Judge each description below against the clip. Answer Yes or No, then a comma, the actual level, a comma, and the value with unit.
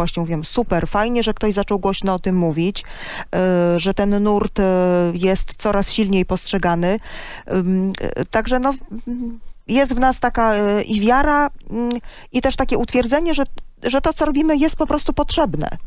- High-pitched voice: Yes, high, 215 Hz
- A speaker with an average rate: No, fast, 180 wpm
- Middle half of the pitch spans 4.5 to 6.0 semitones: Yes, wide, 5.4 semitones